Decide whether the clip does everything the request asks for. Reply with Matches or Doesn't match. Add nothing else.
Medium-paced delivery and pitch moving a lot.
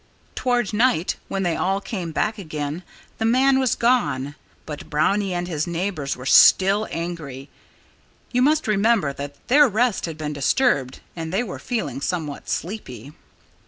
Matches